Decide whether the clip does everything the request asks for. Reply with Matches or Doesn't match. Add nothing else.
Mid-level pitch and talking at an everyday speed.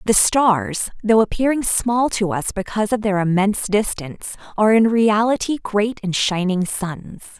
Doesn't match